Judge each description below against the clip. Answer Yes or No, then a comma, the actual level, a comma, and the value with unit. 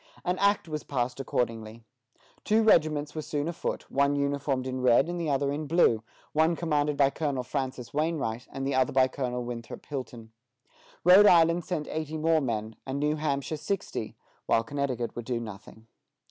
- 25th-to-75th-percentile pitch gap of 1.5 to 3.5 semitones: No, average, 4.0 semitones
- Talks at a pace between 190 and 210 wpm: No, average, 175 wpm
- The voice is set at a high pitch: No, medium, 140 Hz